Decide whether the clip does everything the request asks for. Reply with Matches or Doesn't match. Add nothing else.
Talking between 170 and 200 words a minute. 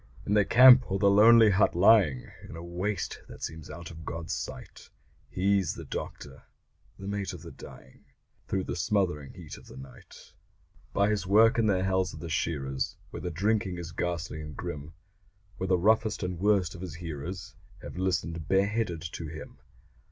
Matches